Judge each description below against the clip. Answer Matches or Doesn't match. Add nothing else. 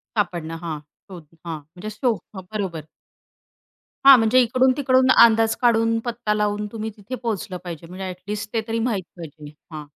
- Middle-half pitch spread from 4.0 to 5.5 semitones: Matches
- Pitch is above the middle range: Matches